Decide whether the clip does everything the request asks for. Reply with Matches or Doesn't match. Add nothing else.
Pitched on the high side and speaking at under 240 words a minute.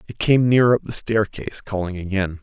Doesn't match